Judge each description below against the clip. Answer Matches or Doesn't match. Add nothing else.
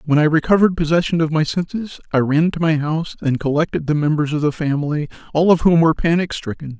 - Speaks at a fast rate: Matches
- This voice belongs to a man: Matches